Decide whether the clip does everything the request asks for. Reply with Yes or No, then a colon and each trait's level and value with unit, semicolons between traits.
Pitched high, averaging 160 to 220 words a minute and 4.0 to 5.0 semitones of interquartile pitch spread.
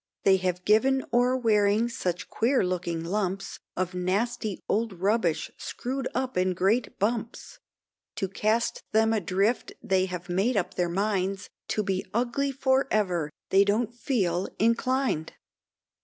No: high, 205 Hz; average, 140 wpm; average, 4.3 semitones